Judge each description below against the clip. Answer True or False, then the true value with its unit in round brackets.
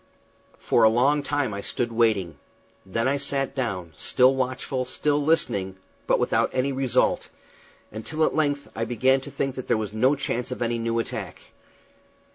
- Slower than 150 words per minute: False (170 wpm)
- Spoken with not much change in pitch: False (3.4 semitones)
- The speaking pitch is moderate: False (125 Hz)